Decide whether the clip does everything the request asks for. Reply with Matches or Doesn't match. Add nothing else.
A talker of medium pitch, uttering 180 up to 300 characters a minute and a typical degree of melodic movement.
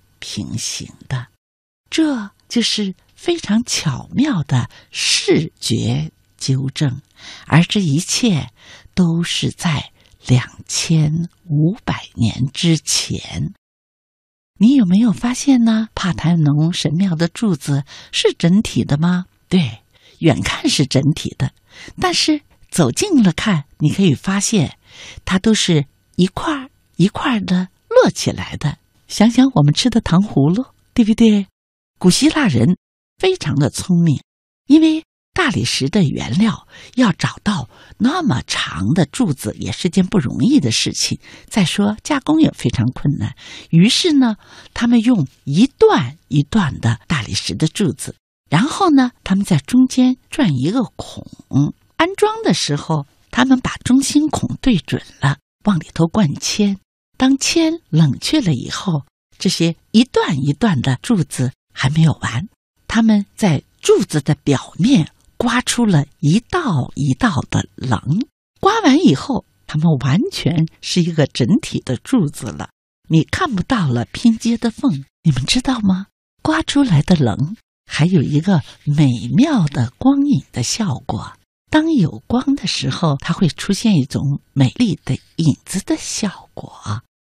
Doesn't match